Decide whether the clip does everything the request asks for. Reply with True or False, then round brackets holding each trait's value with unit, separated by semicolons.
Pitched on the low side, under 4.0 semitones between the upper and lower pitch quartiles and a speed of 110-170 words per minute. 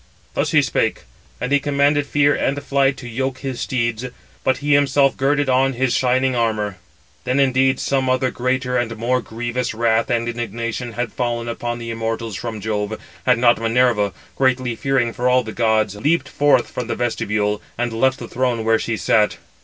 False (125 Hz; 2.4 semitones; 185 wpm)